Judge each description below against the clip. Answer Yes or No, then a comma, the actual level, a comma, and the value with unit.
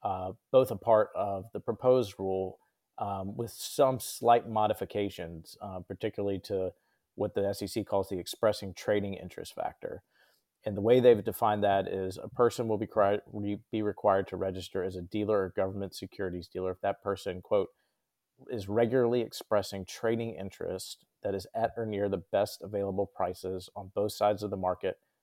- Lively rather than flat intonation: No, narrow, 2.4 semitones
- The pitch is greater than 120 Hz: No, low, 100 Hz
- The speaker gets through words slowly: No, average, 170 wpm